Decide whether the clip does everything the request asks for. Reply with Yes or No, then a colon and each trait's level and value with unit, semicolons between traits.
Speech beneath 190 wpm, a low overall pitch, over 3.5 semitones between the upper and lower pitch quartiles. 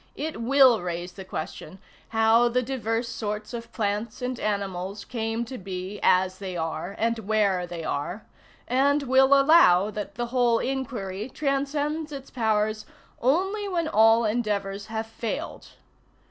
No: average, 145 wpm; high, 225 Hz; average, 4.6 semitones